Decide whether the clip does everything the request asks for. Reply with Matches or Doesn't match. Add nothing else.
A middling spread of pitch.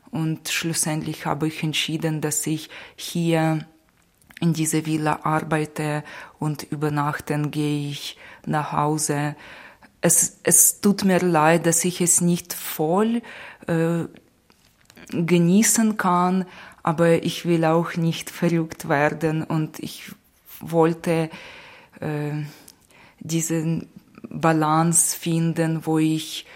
Doesn't match